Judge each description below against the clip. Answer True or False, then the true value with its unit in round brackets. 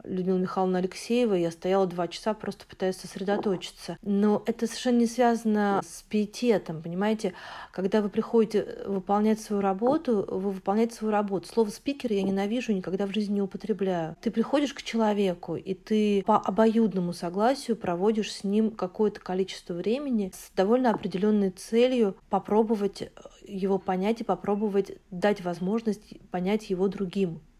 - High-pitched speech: True (205 Hz)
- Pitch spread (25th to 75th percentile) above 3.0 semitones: False (2.7 semitones)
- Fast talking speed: False (145 wpm)